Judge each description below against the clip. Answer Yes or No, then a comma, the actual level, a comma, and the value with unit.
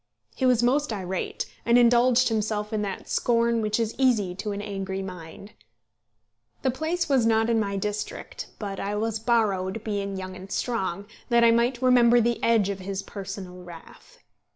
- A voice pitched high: Yes, high, 215 Hz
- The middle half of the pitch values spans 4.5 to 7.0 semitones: No, average, 3.3 semitones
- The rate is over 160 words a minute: Yes, average, 175 wpm